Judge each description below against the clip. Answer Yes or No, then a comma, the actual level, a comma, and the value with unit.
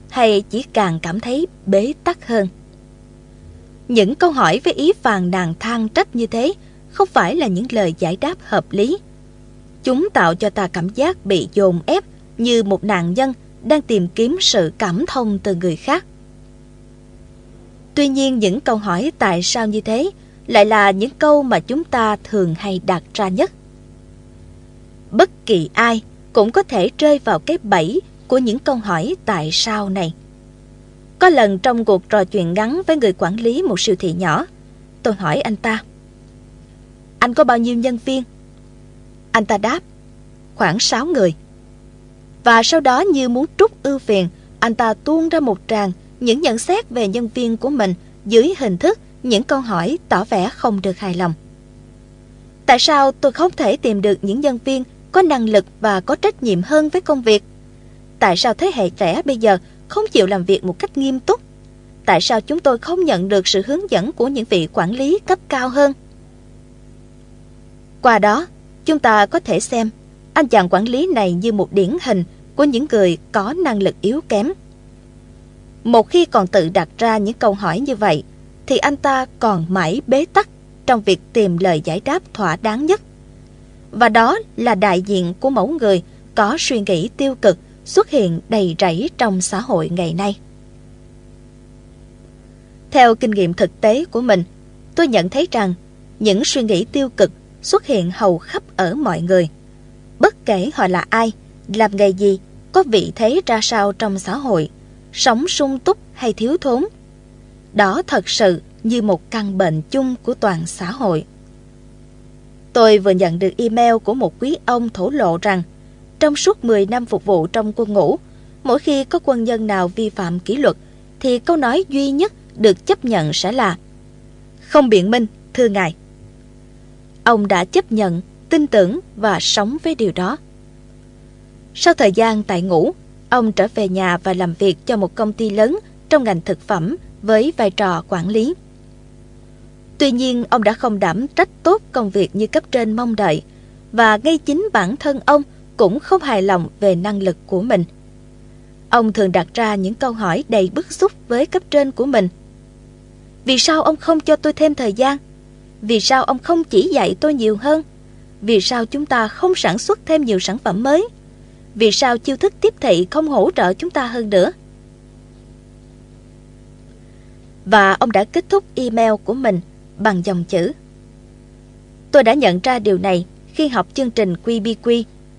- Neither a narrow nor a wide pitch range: No, wide, 6.1 semitones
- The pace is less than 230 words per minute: Yes, average, 180 wpm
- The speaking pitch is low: No, high, 225 Hz